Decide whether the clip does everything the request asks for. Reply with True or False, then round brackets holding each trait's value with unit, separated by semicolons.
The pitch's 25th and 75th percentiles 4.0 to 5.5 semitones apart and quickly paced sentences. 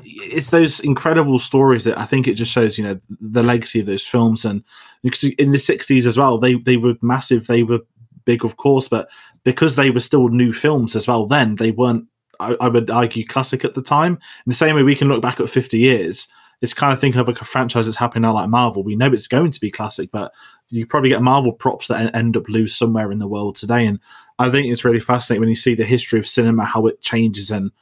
False (2.6 semitones; 250 wpm)